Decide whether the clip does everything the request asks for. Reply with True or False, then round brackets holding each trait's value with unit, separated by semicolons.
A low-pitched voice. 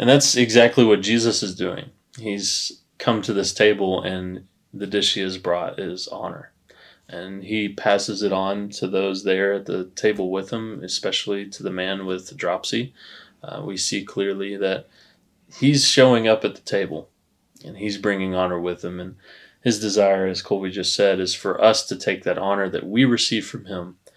True (100 Hz)